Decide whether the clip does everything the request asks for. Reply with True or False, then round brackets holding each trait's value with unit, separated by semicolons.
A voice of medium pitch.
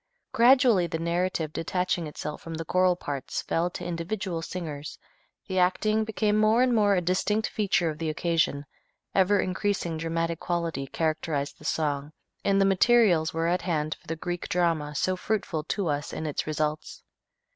True (170 Hz)